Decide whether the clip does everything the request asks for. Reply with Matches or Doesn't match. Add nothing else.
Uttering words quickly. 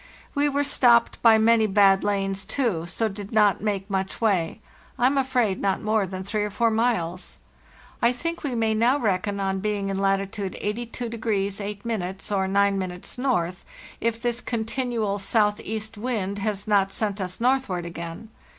Doesn't match